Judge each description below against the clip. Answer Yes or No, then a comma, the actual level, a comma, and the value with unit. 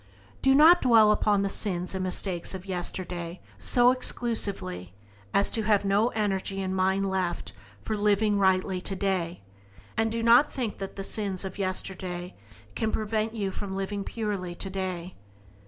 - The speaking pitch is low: No, high, 195 Hz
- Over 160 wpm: No, average, 155 wpm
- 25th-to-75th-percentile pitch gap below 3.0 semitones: Yes, narrow, 2.5 semitones